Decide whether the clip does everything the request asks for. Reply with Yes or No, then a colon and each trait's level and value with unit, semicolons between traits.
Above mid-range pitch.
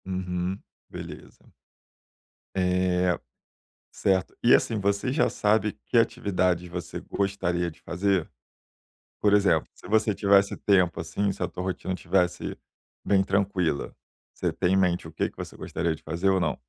No: very low, 95 Hz